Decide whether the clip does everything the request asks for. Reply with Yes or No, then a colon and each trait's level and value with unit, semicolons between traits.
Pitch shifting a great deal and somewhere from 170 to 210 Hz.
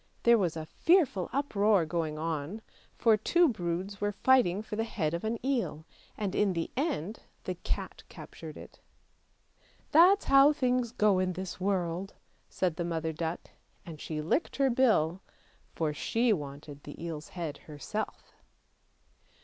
Yes: wide, 6.2 semitones; high, 190 Hz